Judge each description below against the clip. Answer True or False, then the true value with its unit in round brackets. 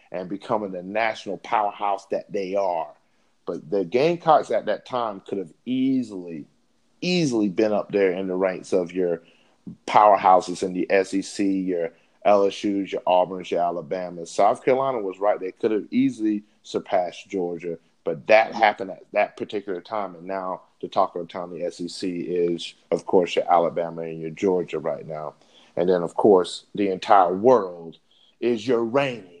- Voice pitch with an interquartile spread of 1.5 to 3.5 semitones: False (4.0 semitones)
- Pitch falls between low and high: False (95 Hz)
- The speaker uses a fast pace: False (165 wpm)